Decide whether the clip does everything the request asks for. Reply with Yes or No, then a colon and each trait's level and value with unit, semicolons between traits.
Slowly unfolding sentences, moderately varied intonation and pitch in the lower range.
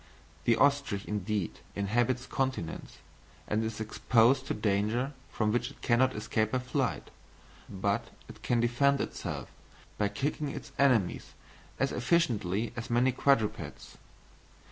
Yes: slow, 125 wpm; average, 3.6 semitones; low, 120 Hz